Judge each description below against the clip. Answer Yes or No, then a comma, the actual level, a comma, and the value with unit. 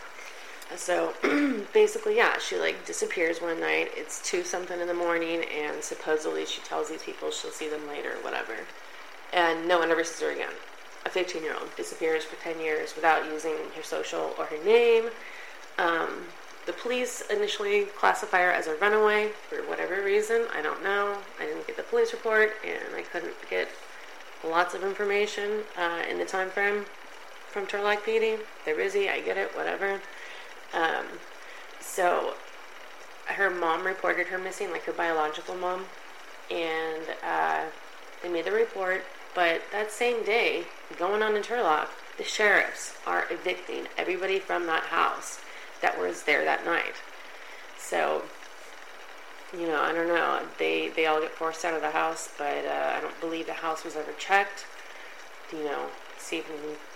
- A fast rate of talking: No, average, 165 wpm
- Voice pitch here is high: Yes, high, 205 Hz